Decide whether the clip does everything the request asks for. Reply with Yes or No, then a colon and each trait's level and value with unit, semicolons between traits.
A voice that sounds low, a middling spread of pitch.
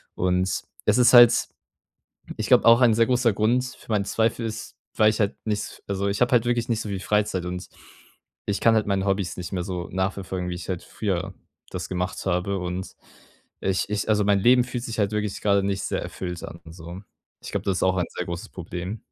Yes: low, 100 Hz; average, 3.3 semitones